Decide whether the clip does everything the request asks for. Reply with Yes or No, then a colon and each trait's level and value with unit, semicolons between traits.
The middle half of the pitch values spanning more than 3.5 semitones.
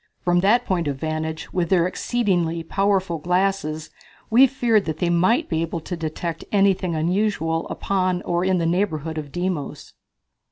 No: average, 3.2 semitones